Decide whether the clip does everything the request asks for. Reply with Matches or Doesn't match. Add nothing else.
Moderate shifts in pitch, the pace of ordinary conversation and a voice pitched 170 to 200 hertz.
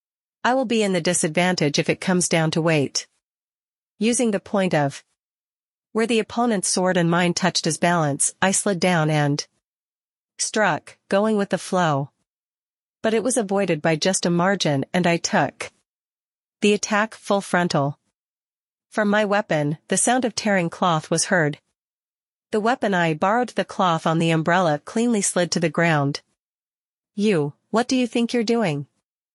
Matches